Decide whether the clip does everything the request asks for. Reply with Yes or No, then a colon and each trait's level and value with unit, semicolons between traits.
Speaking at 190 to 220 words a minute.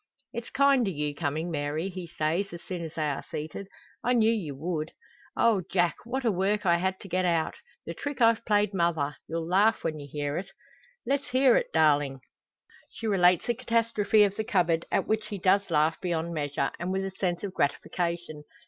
Yes: average, 200 wpm